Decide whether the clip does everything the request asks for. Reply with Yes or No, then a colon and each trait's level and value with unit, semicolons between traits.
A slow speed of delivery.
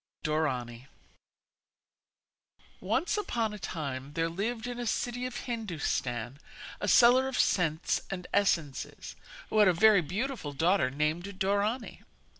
Yes: slow, 125 wpm